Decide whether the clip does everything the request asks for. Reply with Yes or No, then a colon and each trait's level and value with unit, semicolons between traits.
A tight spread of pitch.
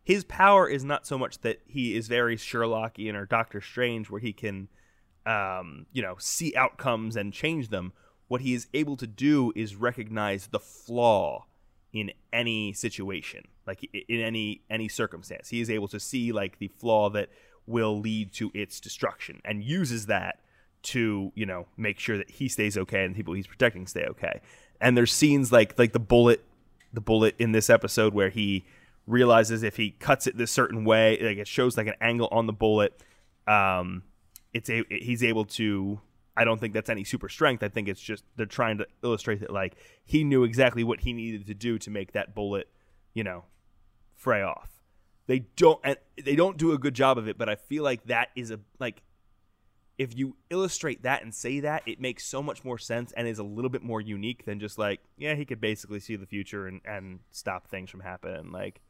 No: average, 3.0 semitones